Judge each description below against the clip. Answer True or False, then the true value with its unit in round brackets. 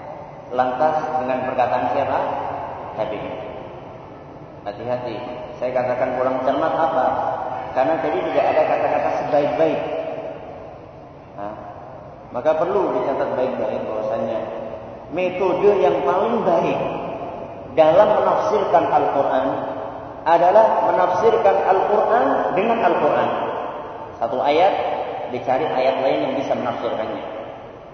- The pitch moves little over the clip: False (4.6 semitones)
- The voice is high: False (135 Hz)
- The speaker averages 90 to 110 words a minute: True (95 wpm)